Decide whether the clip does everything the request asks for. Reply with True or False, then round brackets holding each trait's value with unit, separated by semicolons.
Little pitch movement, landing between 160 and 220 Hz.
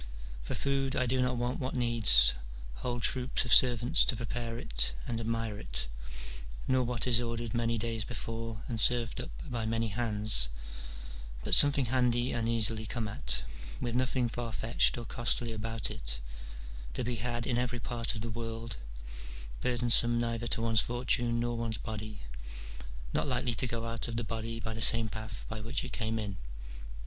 False (1.4 semitones; 115 Hz)